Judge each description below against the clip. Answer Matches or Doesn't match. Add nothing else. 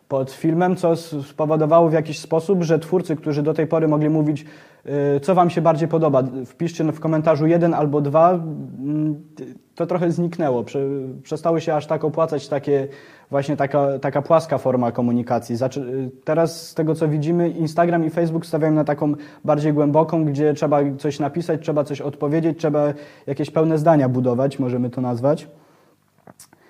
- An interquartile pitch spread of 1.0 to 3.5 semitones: Matches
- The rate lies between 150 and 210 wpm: Matches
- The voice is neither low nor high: Matches